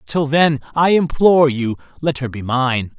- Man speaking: Yes, male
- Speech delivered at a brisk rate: No, average, 180 wpm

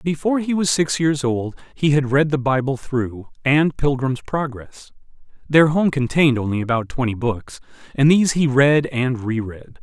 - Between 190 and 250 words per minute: No, average, 175 wpm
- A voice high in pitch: No, low, 135 Hz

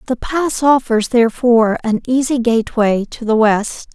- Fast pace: No, average, 150 wpm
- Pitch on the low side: No, high, 235 Hz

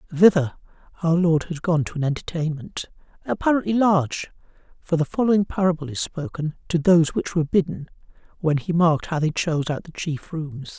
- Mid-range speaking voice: Yes, medium, 165 Hz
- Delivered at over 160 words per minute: Yes, average, 170 wpm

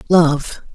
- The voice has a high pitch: No, medium, 160 Hz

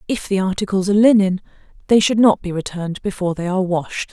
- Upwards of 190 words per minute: Yes, fast, 205 wpm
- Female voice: Yes, female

